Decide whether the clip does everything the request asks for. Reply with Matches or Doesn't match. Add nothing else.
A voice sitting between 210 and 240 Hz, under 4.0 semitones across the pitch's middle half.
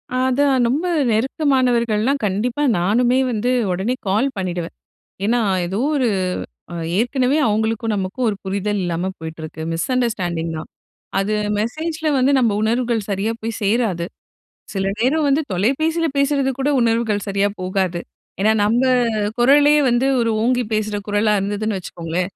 Doesn't match